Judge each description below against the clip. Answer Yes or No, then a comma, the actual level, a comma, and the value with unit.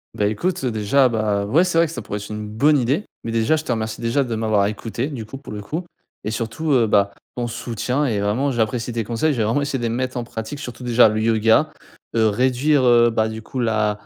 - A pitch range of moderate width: Yes, average, 3.4 semitones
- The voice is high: No, low, 115 Hz